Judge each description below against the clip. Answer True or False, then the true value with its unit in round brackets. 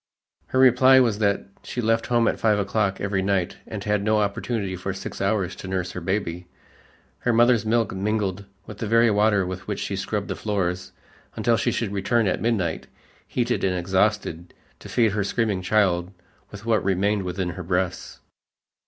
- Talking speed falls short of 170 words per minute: False (180 wpm)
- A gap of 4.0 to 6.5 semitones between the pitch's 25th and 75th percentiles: False (3.1 semitones)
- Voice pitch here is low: True (100 Hz)